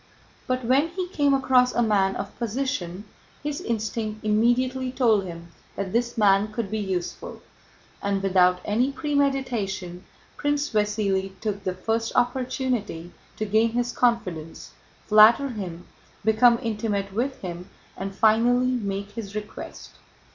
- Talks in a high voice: Yes, high, 220 Hz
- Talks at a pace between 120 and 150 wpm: Yes, slow, 135 wpm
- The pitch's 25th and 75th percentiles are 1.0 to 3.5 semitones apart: No, average, 4.2 semitones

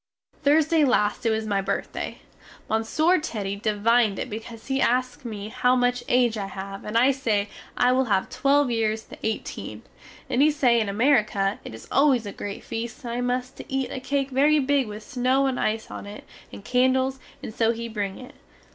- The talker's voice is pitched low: No, high, 235 Hz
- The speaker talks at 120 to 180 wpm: No, average, 200 wpm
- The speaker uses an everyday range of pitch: Yes, average, 3.7 semitones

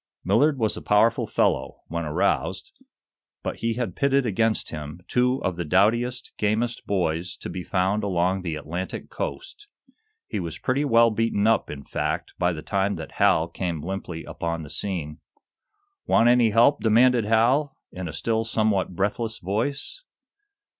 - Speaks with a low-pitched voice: Yes, low, 105 Hz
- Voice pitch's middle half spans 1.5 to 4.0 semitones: No, average, 4.9 semitones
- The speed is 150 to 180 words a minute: Yes, average, 160 wpm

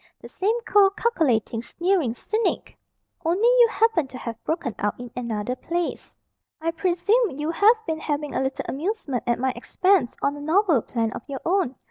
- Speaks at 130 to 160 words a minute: No, average, 175 wpm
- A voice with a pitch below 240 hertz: No, very high, 320 Hz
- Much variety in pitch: Yes, wide, 7.7 semitones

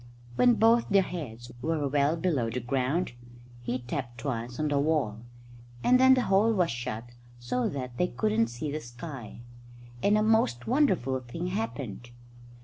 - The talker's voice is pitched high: No, medium, 140 Hz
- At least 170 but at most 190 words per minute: No, average, 160 wpm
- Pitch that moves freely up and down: Yes, wide, 7.1 semitones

